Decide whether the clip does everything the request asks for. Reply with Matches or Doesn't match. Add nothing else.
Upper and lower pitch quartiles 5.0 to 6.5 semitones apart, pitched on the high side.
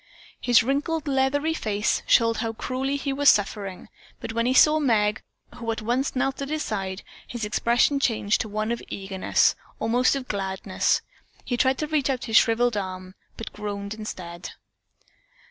Doesn't match